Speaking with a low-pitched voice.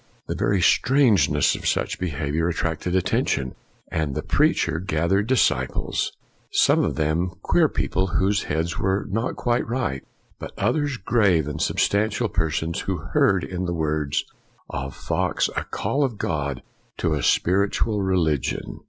Yes: very low, 90 Hz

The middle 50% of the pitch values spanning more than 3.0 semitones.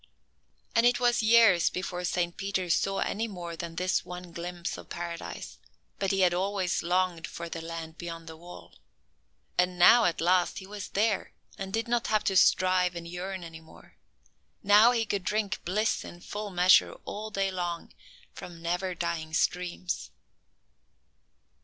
No: narrow, 2.6 semitones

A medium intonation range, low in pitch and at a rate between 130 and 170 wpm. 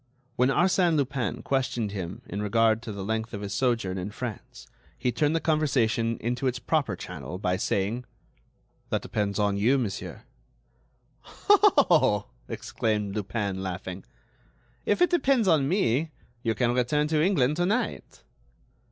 No: wide, 6.6 semitones; low, 120 Hz; average, 145 wpm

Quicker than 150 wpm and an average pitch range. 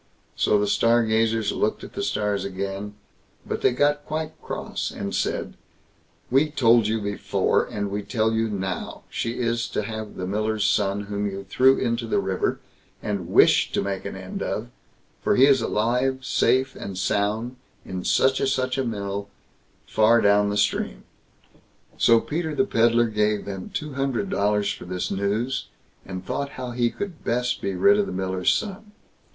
Yes: average, 175 wpm; average, 4.1 semitones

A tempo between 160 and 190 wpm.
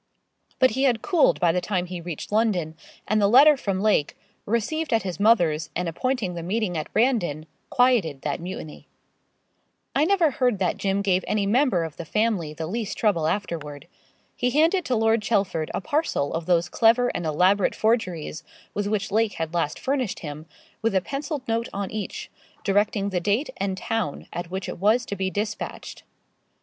Yes: average, 185 wpm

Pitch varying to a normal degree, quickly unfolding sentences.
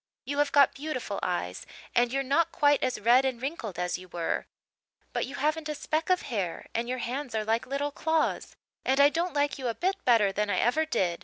Yes: average, 4.7 semitones; fast, 225 wpm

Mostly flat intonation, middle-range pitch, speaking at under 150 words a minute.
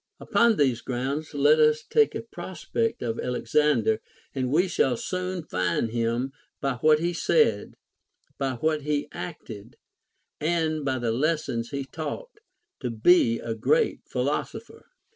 No: average, 4.9 semitones; medium, 145 Hz; average, 140 wpm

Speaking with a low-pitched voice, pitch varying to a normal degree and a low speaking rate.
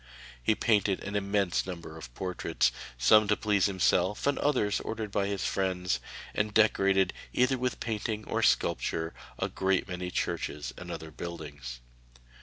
No: very low, 95 Hz; average, 3.2 semitones; average, 150 wpm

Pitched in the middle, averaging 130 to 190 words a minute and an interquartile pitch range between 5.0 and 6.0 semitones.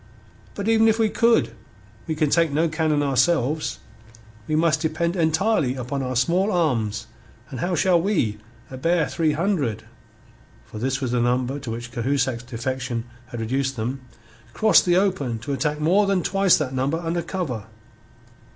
Yes: medium, 150 Hz; average, 165 wpm; average, 5.3 semitones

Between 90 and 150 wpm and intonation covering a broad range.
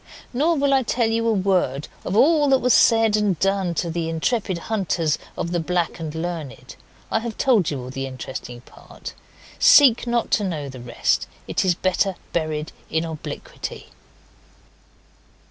No: average, 165 wpm; wide, 6.3 semitones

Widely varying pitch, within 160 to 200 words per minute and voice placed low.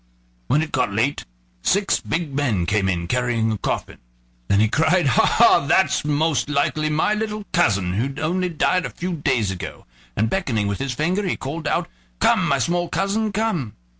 No: wide, 7.9 semitones; average, 185 wpm; medium, 145 Hz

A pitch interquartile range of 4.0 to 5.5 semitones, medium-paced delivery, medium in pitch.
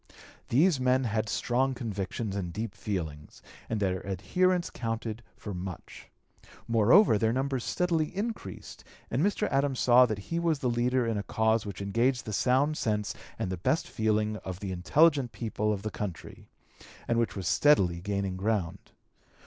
No: average, 4.8 semitones; average, 165 wpm; low, 115 Hz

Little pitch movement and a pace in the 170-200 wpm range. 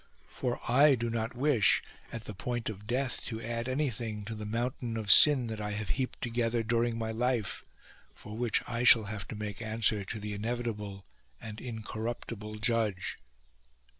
Yes: narrow, 2.1 semitones; average, 175 wpm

